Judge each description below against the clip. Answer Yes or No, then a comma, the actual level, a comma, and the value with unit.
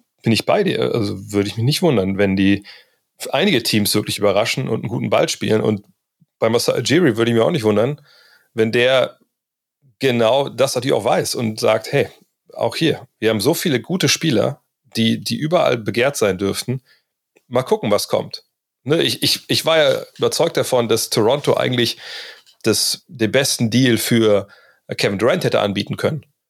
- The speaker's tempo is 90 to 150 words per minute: No, average, 180 wpm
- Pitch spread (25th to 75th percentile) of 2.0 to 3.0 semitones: No, average, 4.2 semitones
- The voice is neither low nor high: No, low, 115 Hz